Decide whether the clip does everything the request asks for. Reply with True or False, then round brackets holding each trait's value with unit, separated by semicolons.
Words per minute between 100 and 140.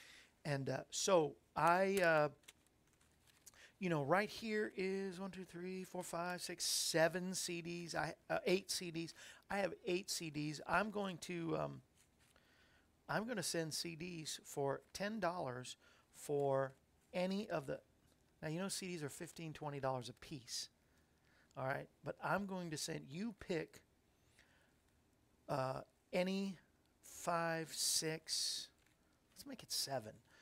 True (135 wpm)